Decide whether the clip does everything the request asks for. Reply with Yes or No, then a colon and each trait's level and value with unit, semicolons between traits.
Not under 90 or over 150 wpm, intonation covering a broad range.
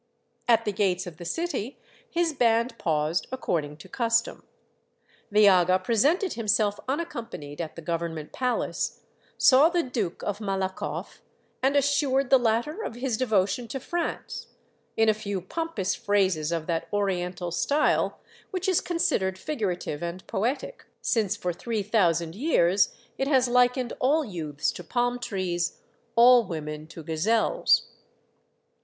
Yes: average, 140 wpm; wide, 6.4 semitones